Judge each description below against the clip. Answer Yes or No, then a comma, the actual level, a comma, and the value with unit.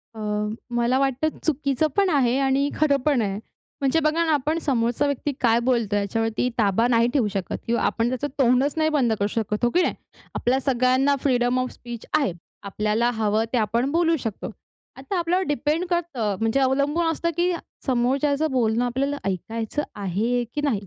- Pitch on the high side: Yes, very high, 255 Hz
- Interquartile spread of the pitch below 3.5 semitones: No, average, 4.2 semitones